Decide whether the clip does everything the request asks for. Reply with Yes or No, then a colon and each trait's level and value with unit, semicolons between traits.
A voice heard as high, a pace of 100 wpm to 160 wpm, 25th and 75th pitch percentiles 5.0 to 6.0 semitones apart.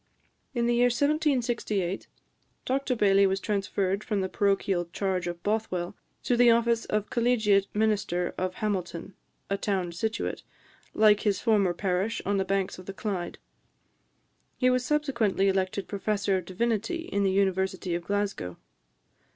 No: high, 200 Hz; average, 145 wpm; average, 3.3 semitones